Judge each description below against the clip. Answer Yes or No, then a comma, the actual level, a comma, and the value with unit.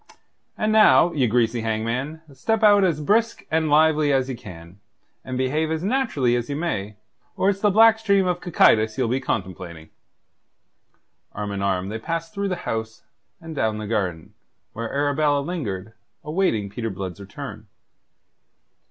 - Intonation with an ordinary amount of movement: No, wide, 7.5 semitones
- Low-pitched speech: Yes, low, 130 Hz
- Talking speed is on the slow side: No, average, 160 wpm